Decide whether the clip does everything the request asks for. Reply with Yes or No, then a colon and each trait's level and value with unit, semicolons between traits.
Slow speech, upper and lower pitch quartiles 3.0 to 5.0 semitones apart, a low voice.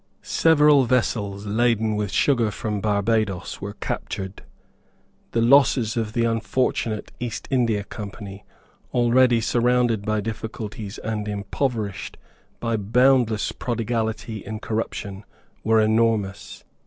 No: slow, 105 wpm; narrow, 2.4 semitones; low, 110 Hz